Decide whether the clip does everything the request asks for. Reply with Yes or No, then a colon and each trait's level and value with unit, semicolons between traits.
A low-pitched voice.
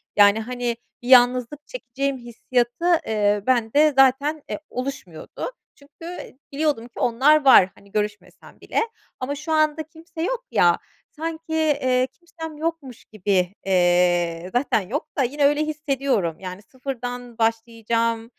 No: very high, 255 Hz